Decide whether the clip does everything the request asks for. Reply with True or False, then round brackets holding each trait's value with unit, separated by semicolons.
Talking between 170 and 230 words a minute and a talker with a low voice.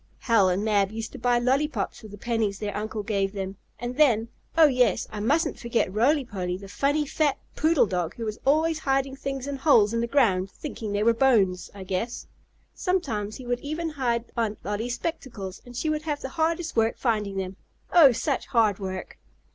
False (200 wpm; 235 Hz)